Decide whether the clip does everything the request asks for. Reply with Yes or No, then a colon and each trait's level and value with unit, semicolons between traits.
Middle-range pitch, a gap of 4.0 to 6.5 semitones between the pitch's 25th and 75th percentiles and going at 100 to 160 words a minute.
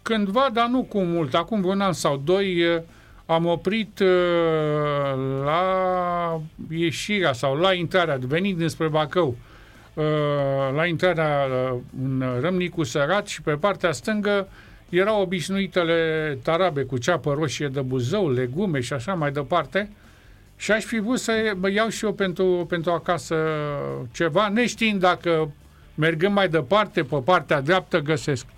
Yes: medium, 170 Hz; average, 4.6 semitones; average, 135 wpm